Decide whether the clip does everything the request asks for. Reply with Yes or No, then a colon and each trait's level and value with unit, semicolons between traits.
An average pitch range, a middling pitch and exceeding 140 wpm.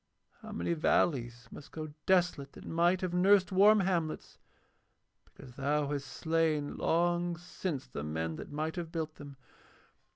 Yes: average, 3.7 semitones; medium, 160 Hz; average, 150 wpm